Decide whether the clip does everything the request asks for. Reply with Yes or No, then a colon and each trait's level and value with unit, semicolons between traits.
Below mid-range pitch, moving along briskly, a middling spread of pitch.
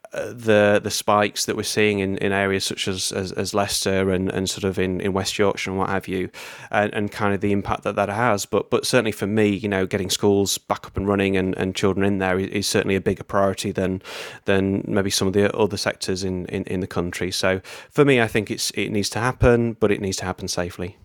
No: low, 100 Hz; fast, 250 wpm; narrow, 1.6 semitones